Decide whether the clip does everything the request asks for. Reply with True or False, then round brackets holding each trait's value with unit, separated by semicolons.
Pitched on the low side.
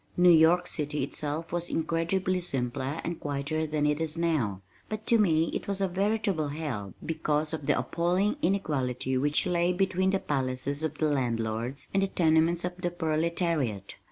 False (160 Hz)